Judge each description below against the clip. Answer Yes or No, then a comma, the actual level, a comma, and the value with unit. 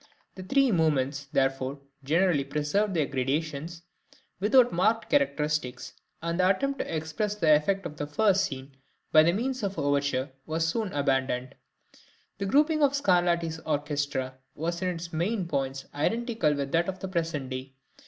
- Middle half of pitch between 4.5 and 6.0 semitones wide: Yes, wide, 5.5 semitones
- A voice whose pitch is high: No, medium, 160 Hz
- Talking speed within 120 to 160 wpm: Yes, average, 155 wpm